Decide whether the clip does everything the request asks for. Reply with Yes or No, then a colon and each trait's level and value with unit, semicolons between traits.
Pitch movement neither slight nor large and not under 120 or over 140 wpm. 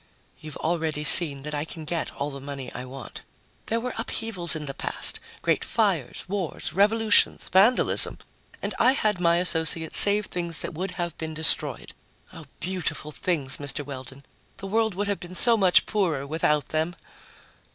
No: average, 4.6 semitones; average, 170 wpm